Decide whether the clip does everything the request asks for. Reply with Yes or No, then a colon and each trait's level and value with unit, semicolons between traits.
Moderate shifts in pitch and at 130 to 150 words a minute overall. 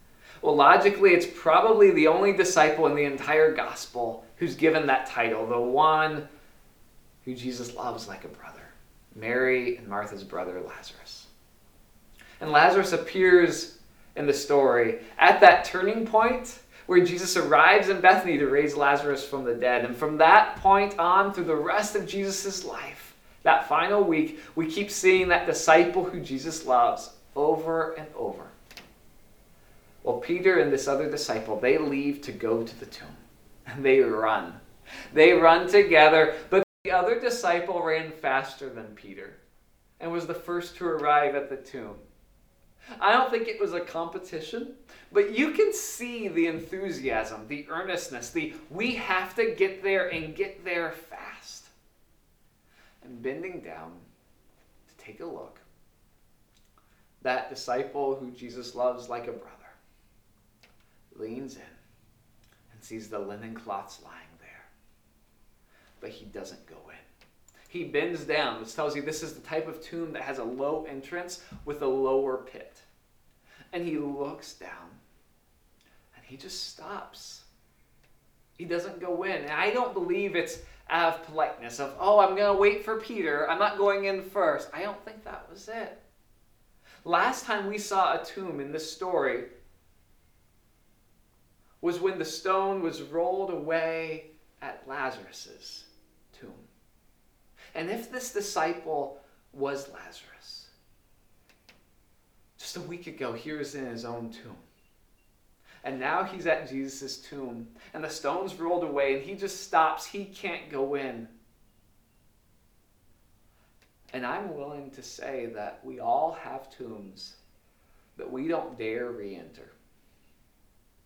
No: wide, 6.6 semitones; average, 145 wpm